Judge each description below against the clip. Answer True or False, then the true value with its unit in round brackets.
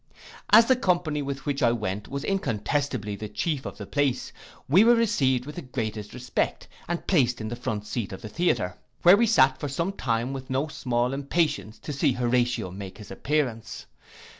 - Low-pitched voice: True (130 Hz)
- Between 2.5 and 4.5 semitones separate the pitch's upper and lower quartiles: False (4.9 semitones)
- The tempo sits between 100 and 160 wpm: False (190 wpm)